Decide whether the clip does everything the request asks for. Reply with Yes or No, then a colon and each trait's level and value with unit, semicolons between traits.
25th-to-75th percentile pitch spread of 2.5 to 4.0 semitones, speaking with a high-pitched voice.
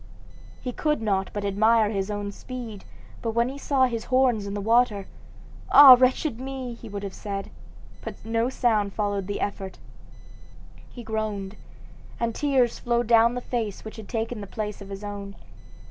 Yes: average, 3.2 semitones; high, 220 Hz